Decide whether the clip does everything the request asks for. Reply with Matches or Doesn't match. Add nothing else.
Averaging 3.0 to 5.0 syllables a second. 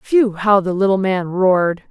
Matches